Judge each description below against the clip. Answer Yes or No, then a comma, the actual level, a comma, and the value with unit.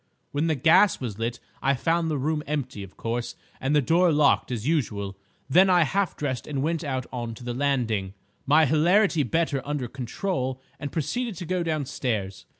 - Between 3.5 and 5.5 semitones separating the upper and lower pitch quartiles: Yes, average, 4.8 semitones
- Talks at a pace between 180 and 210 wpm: Yes, average, 185 wpm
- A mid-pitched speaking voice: Yes, medium, 145 Hz